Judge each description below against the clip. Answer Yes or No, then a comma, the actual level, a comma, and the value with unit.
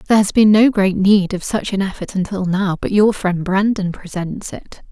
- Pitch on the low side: No, high, 195 Hz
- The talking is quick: Yes, fast, 220 wpm